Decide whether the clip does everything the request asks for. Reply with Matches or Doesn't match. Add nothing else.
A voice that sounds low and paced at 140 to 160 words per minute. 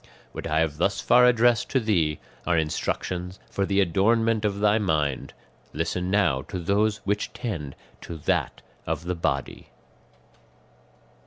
Matches